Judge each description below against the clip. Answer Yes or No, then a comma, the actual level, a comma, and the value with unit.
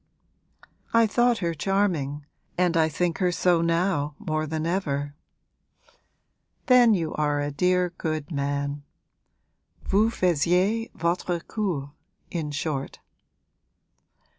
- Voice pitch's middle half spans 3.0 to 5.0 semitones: Yes, average, 4.1 semitones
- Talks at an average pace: No, slow, 110 wpm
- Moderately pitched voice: Yes, medium, 170 Hz